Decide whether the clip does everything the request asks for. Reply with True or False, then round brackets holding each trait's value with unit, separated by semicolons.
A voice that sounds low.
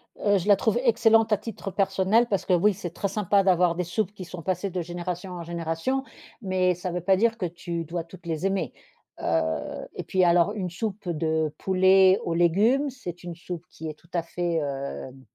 False (180 Hz)